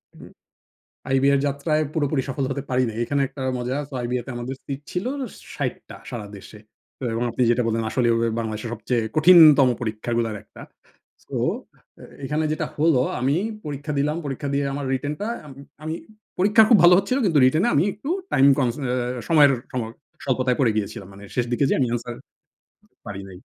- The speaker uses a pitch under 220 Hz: Yes, low, 135 Hz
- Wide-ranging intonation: No, average, 3.8 semitones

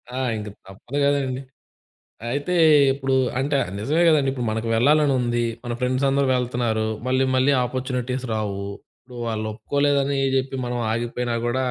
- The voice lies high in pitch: No, low, 130 Hz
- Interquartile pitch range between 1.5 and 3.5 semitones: Yes, average, 2.7 semitones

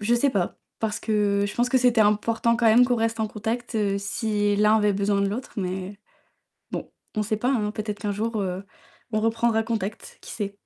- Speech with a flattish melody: Yes, narrow, 2.0 semitones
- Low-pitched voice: No, high, 215 Hz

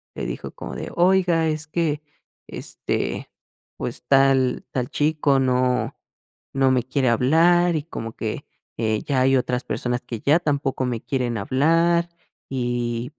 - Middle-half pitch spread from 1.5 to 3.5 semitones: No, average, 4.0 semitones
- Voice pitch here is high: No, low, 135 Hz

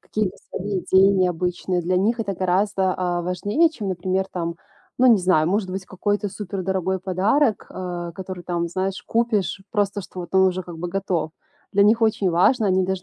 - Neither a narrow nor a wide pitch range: No, narrow, 2.1 semitones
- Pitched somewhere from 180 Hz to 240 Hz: Yes, high, 190 Hz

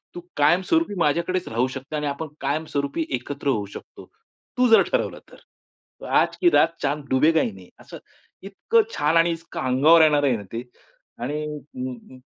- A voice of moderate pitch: Yes, medium, 150 Hz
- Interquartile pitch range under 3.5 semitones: No, average, 4.2 semitones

